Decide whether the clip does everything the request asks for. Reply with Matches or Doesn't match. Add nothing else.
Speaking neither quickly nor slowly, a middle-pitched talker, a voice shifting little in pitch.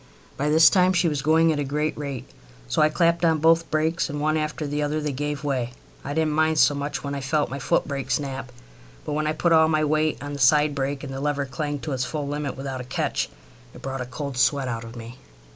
Doesn't match